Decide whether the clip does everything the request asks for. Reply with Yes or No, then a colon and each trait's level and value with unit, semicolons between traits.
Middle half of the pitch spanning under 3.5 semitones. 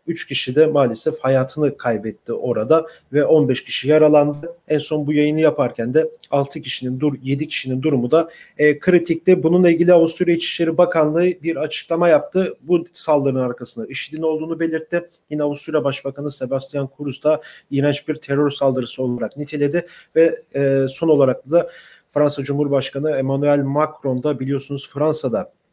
Yes: average, 2.8 semitones